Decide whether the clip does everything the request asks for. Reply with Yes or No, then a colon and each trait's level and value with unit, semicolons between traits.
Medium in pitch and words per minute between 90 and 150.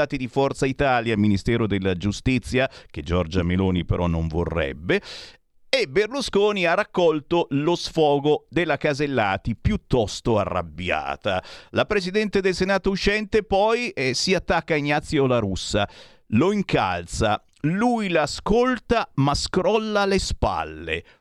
Yes: medium, 145 Hz; average, 120 wpm